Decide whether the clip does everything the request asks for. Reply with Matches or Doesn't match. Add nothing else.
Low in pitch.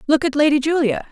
Doesn't match